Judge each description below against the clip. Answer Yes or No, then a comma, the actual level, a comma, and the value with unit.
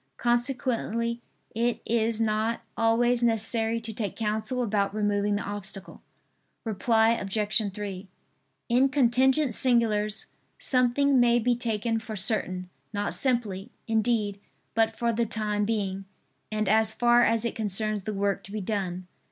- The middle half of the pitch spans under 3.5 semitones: Yes, narrow, 2.4 semitones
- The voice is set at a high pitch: Yes, high, 220 Hz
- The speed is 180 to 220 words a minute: No, slow, 135 wpm